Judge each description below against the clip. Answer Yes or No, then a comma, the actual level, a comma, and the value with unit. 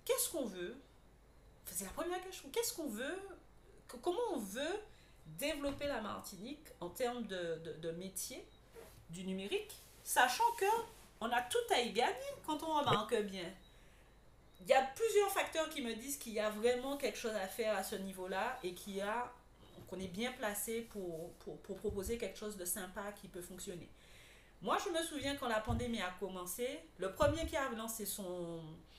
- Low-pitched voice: No, high, 225 Hz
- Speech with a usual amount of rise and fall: No, wide, 7.7 semitones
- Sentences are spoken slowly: No, average, 185 wpm